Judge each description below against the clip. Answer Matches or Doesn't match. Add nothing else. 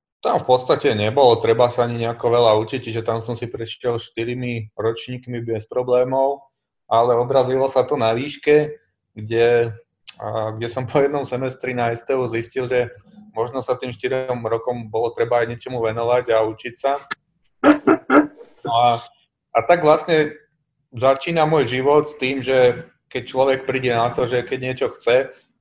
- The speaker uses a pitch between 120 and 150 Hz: Matches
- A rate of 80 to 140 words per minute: Doesn't match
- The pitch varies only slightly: Doesn't match